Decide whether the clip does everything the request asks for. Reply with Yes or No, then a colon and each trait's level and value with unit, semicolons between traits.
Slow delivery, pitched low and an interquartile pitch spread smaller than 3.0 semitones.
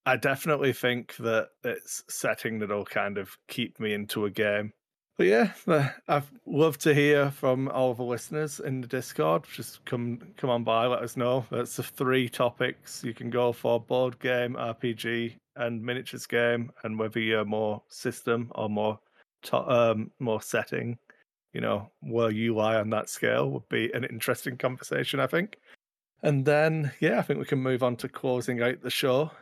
No: average, 185 wpm; low, 120 Hz; narrow, 2.6 semitones